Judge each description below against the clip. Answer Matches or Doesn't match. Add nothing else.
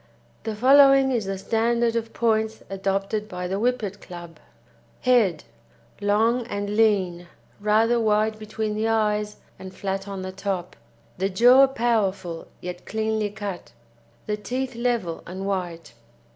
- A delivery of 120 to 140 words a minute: Matches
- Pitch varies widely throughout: Doesn't match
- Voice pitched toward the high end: Matches